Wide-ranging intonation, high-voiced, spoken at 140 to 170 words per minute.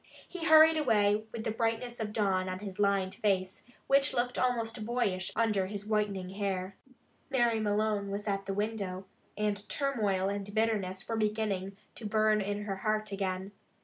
No: narrow, 2.4 semitones; high, 210 Hz; average, 165 wpm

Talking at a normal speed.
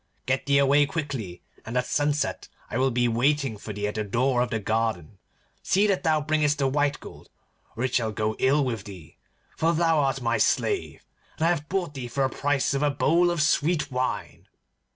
No: fast, 210 wpm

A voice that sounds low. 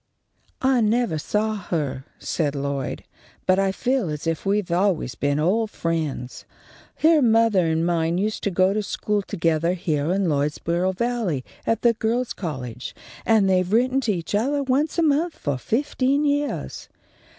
No: high, 195 Hz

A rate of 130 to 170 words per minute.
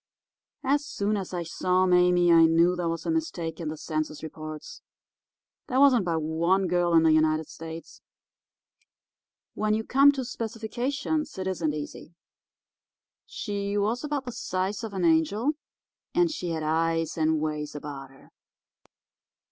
Yes: average, 150 wpm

